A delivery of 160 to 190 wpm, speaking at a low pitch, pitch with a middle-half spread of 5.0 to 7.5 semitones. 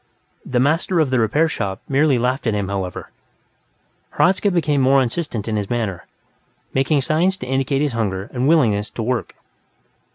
Yes: average, 165 wpm; low, 130 Hz; wide, 5.5 semitones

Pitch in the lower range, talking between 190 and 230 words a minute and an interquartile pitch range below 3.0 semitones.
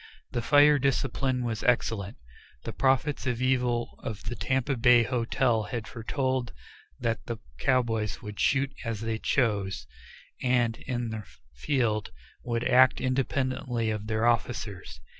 No: low, 120 Hz; slow, 135 wpm; narrow, 2.6 semitones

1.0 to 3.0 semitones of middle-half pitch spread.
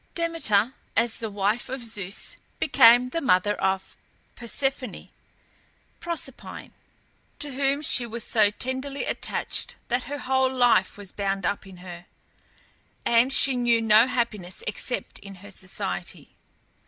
No: average, 4.7 semitones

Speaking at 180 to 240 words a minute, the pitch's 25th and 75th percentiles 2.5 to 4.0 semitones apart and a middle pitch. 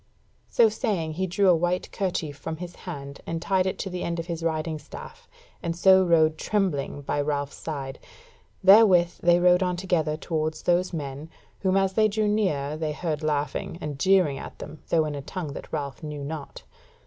Yes: average, 195 wpm; average, 3.5 semitones; medium, 165 Hz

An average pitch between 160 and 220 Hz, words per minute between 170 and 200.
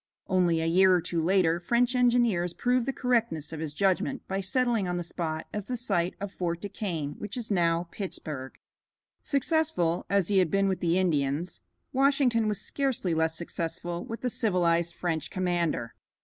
Yes: medium, 185 Hz; average, 175 wpm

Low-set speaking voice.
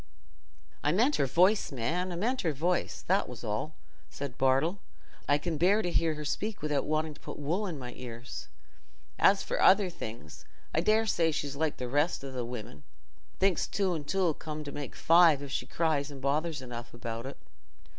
No: medium, 150 Hz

